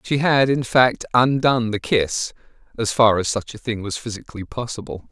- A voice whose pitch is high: No, low, 115 Hz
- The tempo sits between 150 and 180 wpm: No, average, 190 wpm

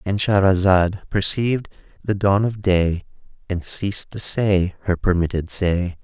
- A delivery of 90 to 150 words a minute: Yes, average, 140 wpm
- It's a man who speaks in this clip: Yes, male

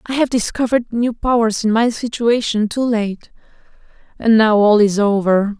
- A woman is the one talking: Yes, female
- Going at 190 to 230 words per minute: No, average, 150 wpm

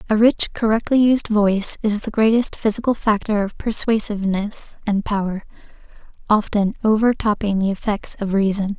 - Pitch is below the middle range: No, high, 210 Hz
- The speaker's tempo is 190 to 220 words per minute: No, average, 145 wpm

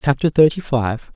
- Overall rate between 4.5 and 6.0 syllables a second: Yes, 4.8 syllables/s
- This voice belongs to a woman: No, male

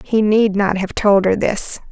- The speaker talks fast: Yes, fast, 220 wpm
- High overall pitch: Yes, high, 205 Hz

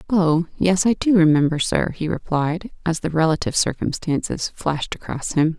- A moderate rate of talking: Yes, average, 160 wpm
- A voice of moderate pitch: Yes, medium, 165 Hz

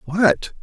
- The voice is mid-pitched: Yes, medium, 165 Hz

